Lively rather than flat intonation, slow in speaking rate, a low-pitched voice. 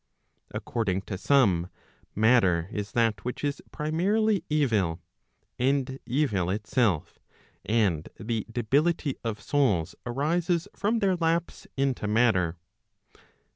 Yes: wide, 6.8 semitones; slow, 105 wpm; low, 120 Hz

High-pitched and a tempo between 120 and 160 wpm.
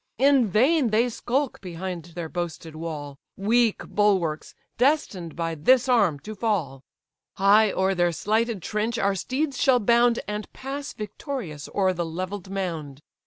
Yes: high, 200 Hz; average, 145 wpm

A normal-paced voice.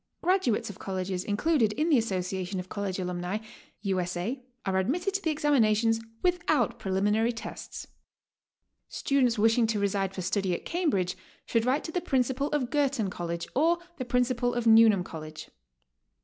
Yes: average, 160 wpm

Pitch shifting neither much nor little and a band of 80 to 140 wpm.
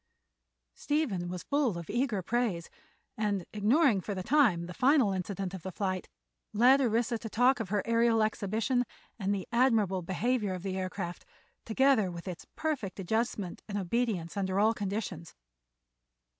No: average, 4.4 semitones; average, 155 wpm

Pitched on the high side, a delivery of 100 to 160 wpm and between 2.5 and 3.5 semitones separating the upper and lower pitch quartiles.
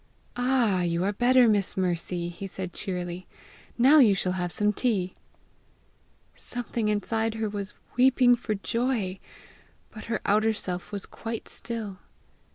No: high, 210 Hz; average, 140 wpm; average, 4.1 semitones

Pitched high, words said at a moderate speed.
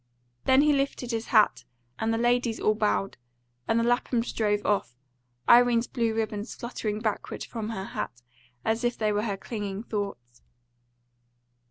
Yes: high, 225 Hz; average, 155 wpm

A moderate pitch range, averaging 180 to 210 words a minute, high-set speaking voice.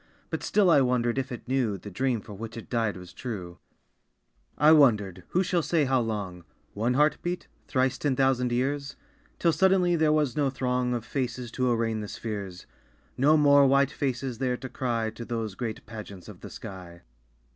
No: average, 4.0 semitones; average, 190 wpm; low, 125 Hz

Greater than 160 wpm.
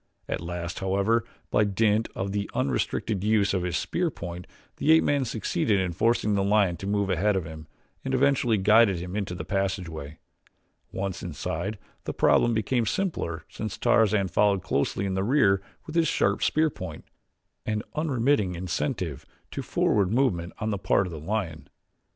Yes: average, 170 wpm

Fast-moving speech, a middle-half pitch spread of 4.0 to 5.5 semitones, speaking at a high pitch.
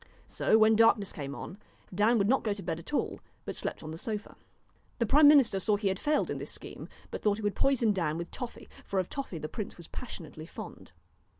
Yes: fast, 230 wpm; average, 4.8 semitones; high, 205 Hz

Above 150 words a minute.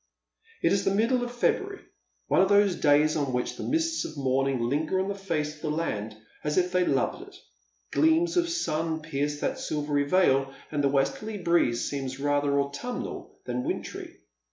Yes: average, 185 wpm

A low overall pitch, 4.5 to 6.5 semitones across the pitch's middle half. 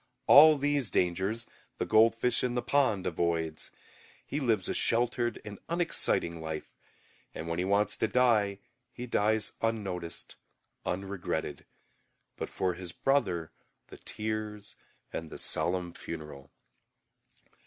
Yes: low, 105 Hz; average, 5.3 semitones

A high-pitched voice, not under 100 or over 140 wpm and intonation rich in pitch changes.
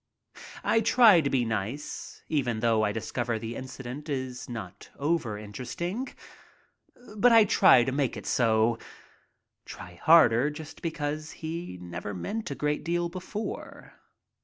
No: low, 135 Hz; slow, 135 wpm; wide, 6.7 semitones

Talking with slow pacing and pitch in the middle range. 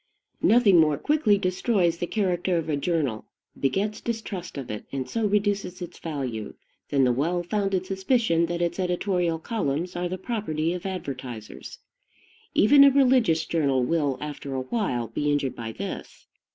No: average, 160 wpm; medium, 175 Hz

